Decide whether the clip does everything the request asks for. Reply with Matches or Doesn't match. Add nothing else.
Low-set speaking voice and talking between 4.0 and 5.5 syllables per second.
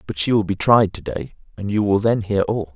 Matches